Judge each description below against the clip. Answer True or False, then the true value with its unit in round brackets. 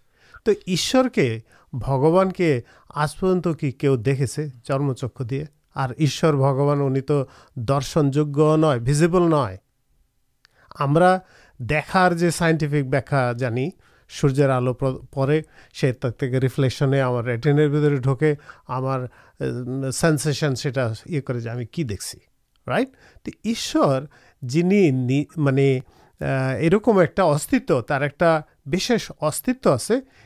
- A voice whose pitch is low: False (145 Hz)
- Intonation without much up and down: False (3.7 semitones)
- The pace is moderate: False (80 wpm)